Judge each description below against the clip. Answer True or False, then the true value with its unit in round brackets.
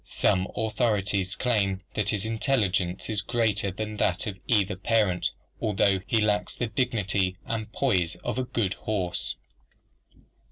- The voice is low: True (105 Hz)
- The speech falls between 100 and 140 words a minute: True (135 wpm)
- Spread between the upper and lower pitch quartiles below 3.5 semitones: True (2.8 semitones)